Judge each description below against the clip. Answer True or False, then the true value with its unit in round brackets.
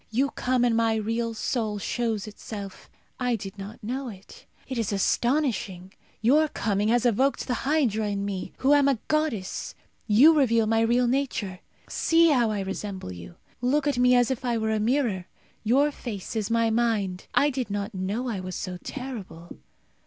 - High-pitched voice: True (230 Hz)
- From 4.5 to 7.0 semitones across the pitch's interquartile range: False (4.0 semitones)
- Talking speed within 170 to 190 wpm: True (180 wpm)